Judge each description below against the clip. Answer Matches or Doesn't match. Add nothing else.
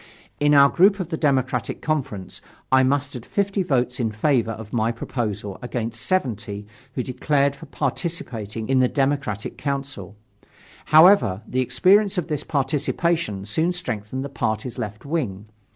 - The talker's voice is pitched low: Matches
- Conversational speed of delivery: Matches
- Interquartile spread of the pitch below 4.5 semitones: Doesn't match